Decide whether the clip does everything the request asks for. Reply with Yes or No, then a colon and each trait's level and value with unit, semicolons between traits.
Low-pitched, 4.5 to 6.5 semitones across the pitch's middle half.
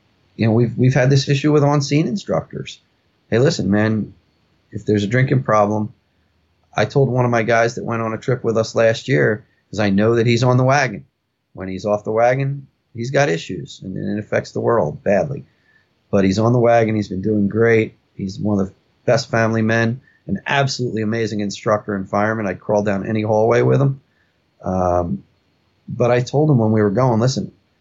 No: low, 110 Hz; average, 3.2 semitones